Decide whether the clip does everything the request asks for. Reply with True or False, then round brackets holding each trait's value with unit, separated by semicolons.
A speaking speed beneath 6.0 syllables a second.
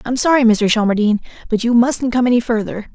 False (6.3 syllables/s)